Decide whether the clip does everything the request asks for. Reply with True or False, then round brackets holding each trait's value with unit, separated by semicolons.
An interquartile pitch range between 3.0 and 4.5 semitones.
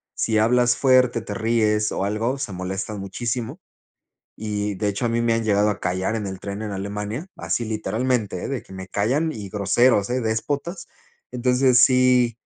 True (3.5 semitones)